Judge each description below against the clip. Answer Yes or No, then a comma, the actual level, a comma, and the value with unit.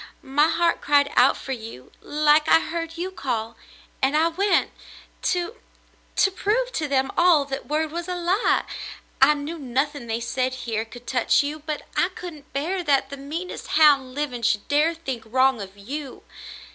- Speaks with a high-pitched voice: Yes, very high, 290 Hz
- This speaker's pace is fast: No, average, 190 wpm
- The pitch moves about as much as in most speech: Yes, average, 4.2 semitones